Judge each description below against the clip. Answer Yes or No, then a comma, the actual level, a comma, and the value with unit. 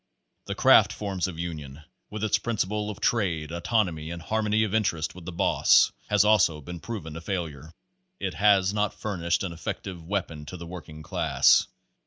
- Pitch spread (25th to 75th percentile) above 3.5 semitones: Yes, average, 4.2 semitones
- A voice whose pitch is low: Yes, very low, 90 Hz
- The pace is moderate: Yes, average, 175 wpm